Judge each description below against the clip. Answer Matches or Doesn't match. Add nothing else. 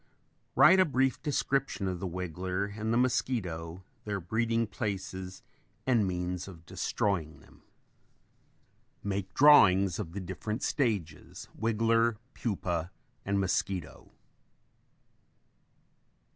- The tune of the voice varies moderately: Matches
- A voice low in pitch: Matches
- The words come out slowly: Matches